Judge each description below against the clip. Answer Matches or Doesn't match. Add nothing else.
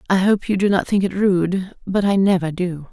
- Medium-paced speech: Doesn't match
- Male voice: Doesn't match